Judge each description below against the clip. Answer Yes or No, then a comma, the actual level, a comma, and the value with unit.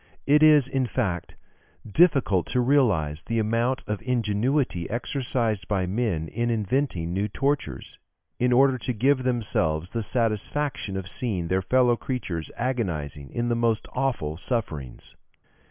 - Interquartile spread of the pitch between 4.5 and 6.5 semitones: Yes, wide, 5.6 semitones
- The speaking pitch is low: Yes, low, 115 Hz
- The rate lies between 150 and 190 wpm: No, average, 140 wpm